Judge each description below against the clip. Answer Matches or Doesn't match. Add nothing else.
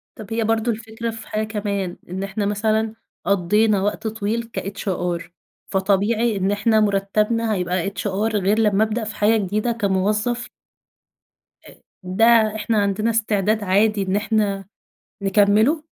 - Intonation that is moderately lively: Doesn't match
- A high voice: Matches